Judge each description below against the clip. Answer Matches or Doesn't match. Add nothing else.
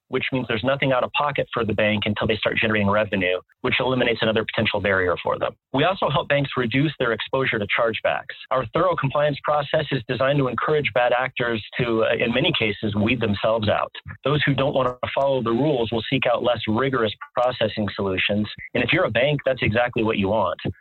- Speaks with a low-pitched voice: Matches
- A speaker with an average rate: Doesn't match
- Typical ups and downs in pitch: Matches